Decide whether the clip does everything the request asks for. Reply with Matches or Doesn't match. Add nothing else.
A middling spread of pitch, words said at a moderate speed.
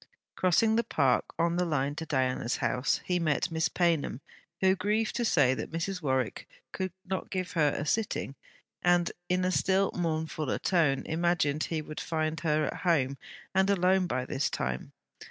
Matches